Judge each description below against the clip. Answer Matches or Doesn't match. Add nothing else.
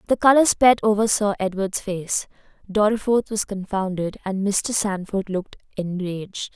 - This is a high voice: Matches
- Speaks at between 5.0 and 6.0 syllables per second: Doesn't match